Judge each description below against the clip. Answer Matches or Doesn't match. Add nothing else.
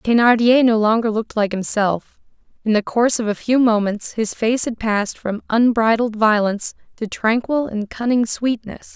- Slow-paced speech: Doesn't match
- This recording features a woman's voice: Matches